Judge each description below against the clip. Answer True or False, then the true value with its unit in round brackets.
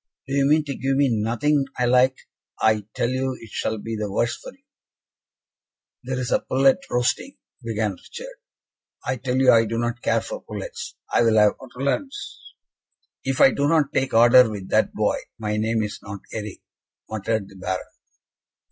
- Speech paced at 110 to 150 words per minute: False (180 wpm)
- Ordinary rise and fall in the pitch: True (3.8 semitones)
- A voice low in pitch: True (120 Hz)